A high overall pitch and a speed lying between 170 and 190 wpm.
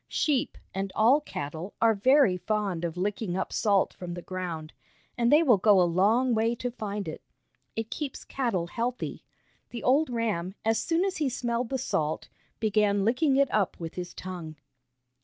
Yes: high, 215 Hz; average, 175 wpm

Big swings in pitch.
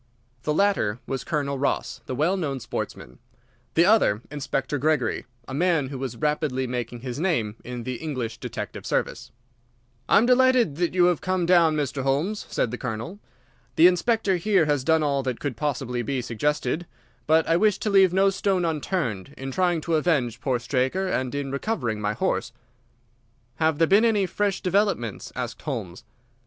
Yes: wide, 6.0 semitones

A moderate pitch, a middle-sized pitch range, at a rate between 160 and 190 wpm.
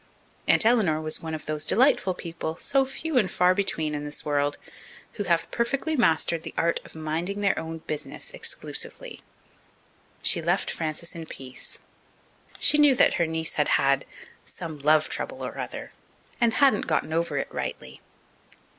Yes: medium, 165 Hz; average, 4.9 semitones; average, 165 wpm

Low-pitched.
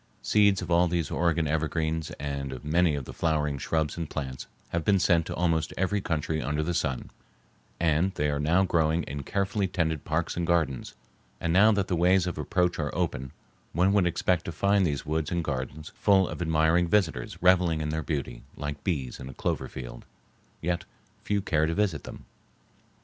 Yes: very low, 80 Hz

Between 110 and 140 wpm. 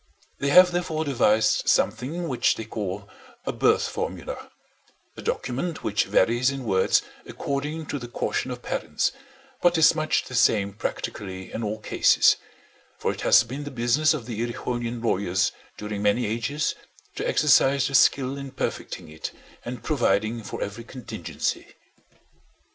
No: average, 150 wpm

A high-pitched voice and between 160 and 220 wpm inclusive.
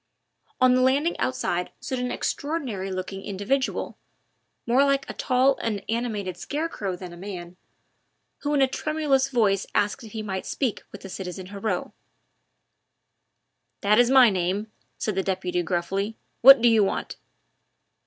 No: high, 215 Hz; average, 150 wpm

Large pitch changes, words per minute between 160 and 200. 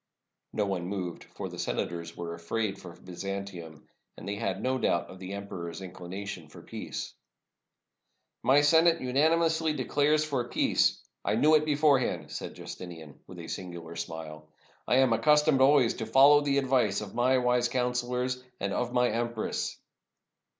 Yes: wide, 6.8 semitones; average, 165 wpm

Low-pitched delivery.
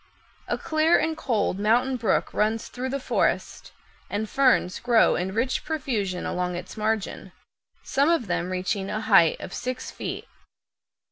No: high, 220 Hz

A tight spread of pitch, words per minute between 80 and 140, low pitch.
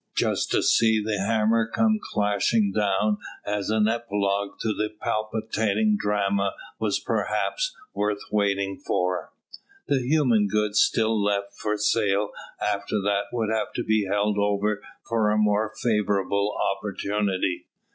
Yes: narrow, 1.5 semitones; slow, 135 wpm; low, 105 Hz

